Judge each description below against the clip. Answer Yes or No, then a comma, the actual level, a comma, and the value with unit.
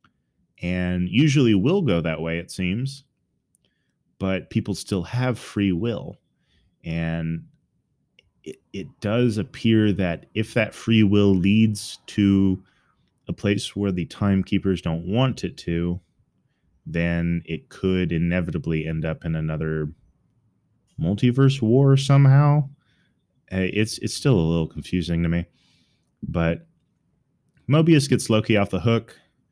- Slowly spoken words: Yes, slow, 125 wpm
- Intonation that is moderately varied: No, wide, 6.0 semitones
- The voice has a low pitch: Yes, low, 100 Hz